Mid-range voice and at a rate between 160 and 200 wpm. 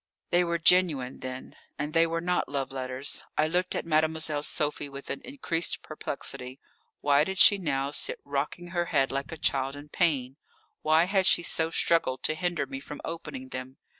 Yes: medium, 150 Hz; average, 185 wpm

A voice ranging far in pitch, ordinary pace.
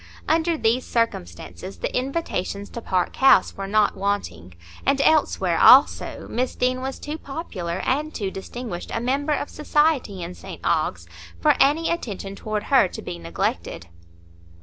Yes: wide, 7.3 semitones; average, 150 wpm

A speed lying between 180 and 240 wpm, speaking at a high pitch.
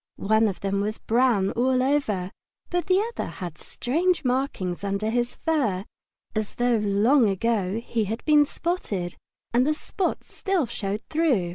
No: average, 155 wpm; high, 230 Hz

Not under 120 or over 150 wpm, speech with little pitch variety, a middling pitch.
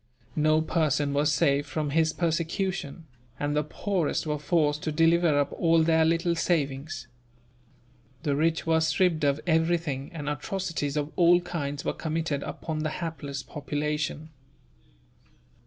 Yes: average, 140 wpm; narrow, 2.2 semitones; medium, 155 Hz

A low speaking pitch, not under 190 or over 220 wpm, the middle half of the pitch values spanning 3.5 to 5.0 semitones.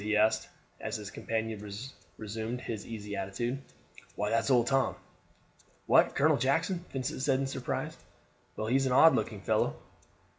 No: low, 115 Hz; average, 155 wpm; average, 4.0 semitones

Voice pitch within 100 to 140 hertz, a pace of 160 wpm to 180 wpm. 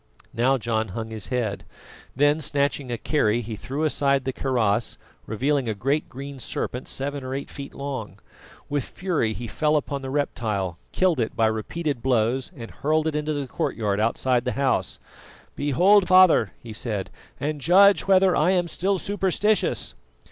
Yes: low, 135 Hz; average, 165 wpm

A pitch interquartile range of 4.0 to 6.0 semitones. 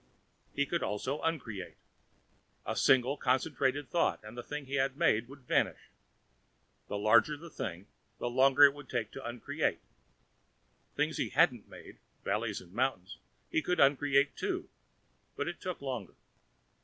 No: average, 3.5 semitones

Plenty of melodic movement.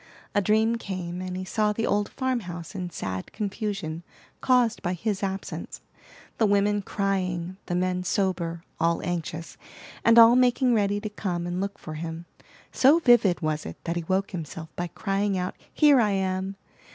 No: average, 3.3 semitones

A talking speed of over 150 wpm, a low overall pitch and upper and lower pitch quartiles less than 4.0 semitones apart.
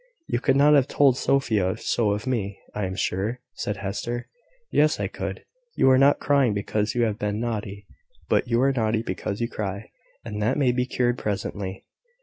Yes: average, 190 wpm; low, 115 Hz; average, 3.6 semitones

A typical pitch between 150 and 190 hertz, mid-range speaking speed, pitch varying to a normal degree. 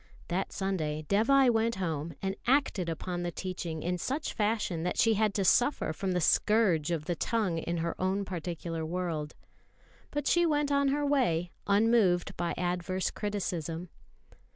Yes: medium, 185 Hz; average, 160 wpm; average, 4.9 semitones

